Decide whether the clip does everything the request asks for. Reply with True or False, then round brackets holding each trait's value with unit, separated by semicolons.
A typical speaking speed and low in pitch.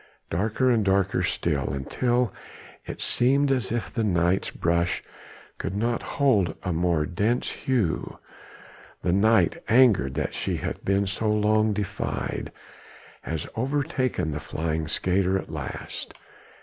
False (130 wpm; 100 Hz)